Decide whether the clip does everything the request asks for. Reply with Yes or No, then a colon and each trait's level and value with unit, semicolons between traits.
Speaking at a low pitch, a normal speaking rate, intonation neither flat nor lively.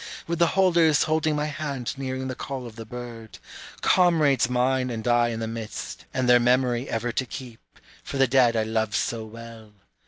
Yes: low, 125 Hz; average, 190 wpm; average, 3.1 semitones